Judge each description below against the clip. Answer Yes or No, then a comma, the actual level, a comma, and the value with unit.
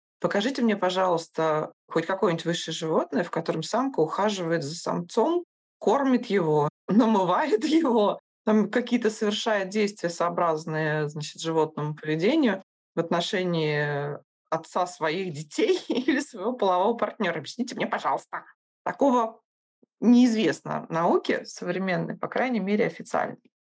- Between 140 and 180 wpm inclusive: No, average, 115 wpm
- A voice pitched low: No, high, 190 Hz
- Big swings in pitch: Yes, wide, 6.3 semitones